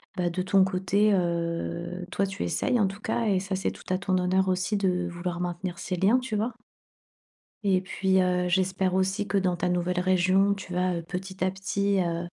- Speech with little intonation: Yes, narrow, 1.4 semitones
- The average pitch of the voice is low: No, medium, 185 Hz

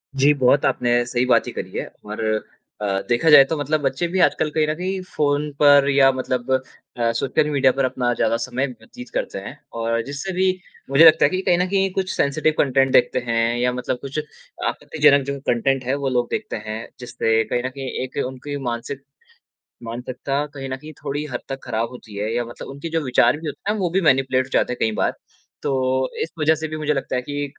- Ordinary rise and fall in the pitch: Yes, average, 3.3 semitones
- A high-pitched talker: No, low, 135 Hz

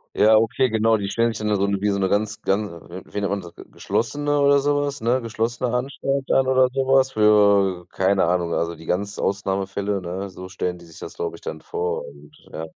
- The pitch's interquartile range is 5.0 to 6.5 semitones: Yes, average, 5.3 semitones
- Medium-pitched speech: No, low, 105 Hz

